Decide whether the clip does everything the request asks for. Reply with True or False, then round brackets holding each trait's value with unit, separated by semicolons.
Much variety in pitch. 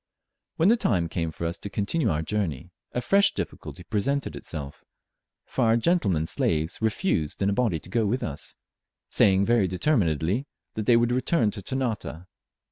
True (6.8 semitones)